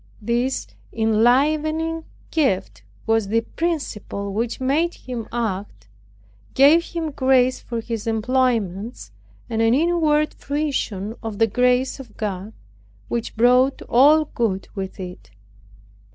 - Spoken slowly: Yes, slow, 115 wpm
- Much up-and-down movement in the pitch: No, average, 4.6 semitones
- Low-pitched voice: No, high, 240 Hz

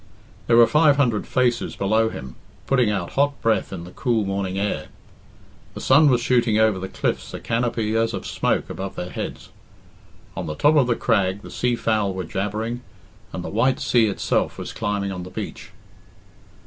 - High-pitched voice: No, low, 110 Hz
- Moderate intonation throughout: Yes, average, 3.9 semitones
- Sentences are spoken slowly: No, average, 185 wpm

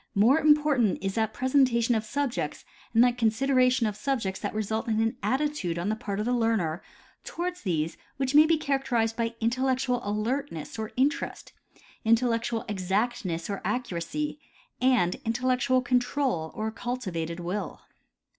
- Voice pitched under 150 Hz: No, high, 230 Hz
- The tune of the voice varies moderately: Yes, average, 3.8 semitones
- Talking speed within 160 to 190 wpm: No, average, 145 wpm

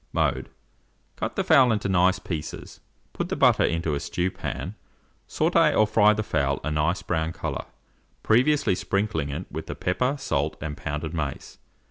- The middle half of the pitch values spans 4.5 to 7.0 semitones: Yes, wide, 5.5 semitones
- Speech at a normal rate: Yes, average, 160 wpm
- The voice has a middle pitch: No, very low, 90 Hz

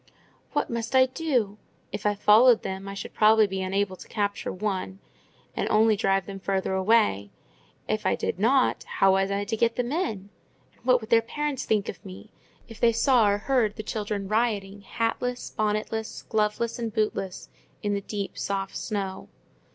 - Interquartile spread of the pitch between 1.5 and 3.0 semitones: Yes, average, 2.7 semitones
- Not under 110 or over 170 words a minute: No, average, 180 wpm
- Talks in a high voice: Yes, high, 210 Hz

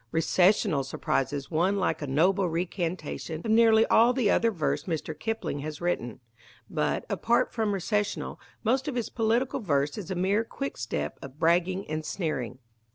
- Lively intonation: Yes, wide, 6.1 semitones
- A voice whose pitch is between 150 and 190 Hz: Yes, medium, 185 Hz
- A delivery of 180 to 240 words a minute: No, average, 160 wpm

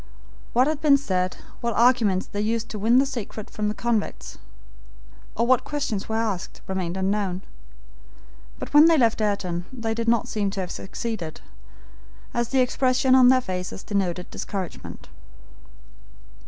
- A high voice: Yes, high, 220 Hz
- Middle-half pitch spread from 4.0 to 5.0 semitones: Yes, average, 4.5 semitones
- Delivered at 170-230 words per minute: No, average, 155 wpm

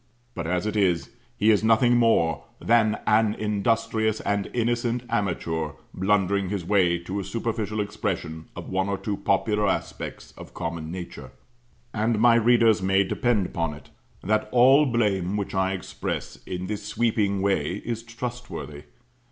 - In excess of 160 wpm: No, average, 150 wpm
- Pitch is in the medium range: No, low, 105 Hz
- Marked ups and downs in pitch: No, average, 3.4 semitones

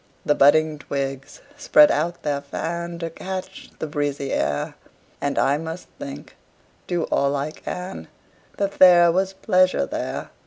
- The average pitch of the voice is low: No, medium, 165 Hz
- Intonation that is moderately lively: Yes, average, 4.3 semitones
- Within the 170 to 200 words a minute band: No, average, 145 wpm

